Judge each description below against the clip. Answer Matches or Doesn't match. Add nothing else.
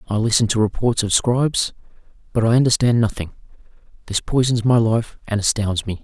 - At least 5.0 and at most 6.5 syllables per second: Matches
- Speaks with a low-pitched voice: Matches